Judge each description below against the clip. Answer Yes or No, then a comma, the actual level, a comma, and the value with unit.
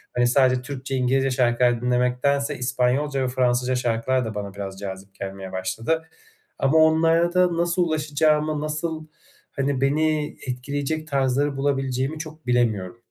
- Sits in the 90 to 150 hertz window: Yes, low, 135 Hz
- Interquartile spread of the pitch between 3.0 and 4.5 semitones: Yes, average, 3.7 semitones